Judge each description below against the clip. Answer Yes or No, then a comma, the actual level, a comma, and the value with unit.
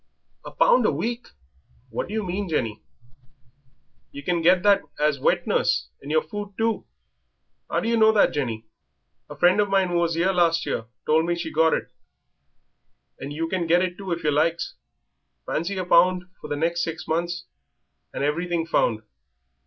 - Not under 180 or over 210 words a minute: Yes, average, 185 wpm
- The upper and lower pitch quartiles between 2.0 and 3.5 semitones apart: Yes, average, 3.0 semitones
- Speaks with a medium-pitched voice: Yes, medium, 170 Hz